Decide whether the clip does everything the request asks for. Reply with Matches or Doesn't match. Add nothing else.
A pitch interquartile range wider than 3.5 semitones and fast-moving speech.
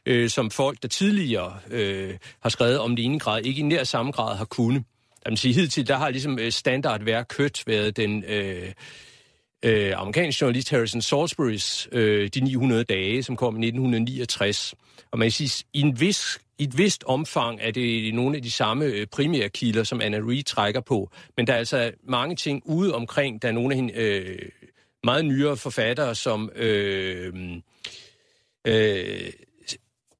Doesn't match